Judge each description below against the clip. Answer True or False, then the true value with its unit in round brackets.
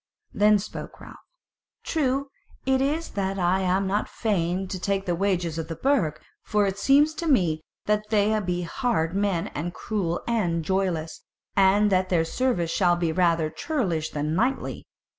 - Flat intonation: False (4.0 semitones)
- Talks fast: False (165 wpm)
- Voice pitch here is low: False (190 Hz)